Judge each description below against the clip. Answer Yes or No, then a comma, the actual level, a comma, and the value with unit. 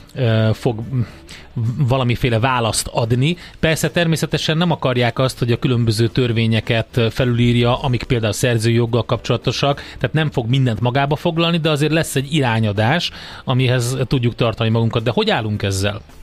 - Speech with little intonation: No, average, 3.5 semitones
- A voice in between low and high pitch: No, low, 125 Hz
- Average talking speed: Yes, average, 140 wpm